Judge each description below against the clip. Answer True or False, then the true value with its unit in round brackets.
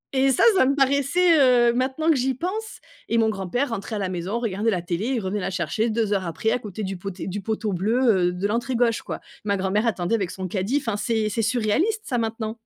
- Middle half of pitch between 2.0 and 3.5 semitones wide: False (4.6 semitones)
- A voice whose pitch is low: False (220 Hz)